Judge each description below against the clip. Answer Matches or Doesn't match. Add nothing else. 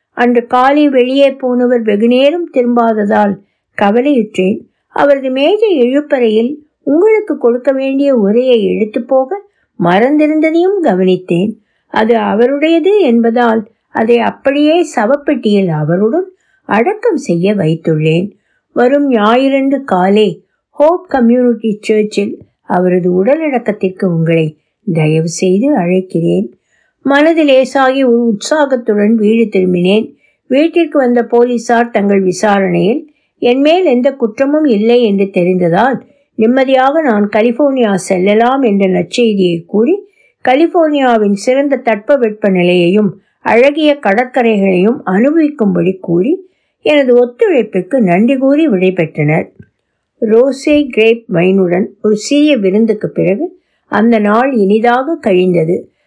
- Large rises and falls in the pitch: Matches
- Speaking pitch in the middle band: Doesn't match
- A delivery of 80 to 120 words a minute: Matches